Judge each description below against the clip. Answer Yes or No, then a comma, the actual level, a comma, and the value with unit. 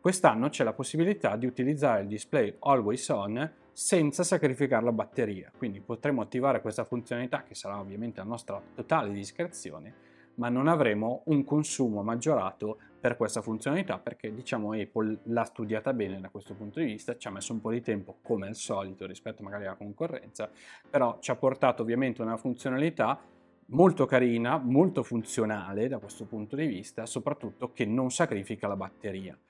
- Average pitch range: Yes, average, 4.5 semitones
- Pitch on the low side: Yes, low, 115 Hz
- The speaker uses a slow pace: No, average, 165 wpm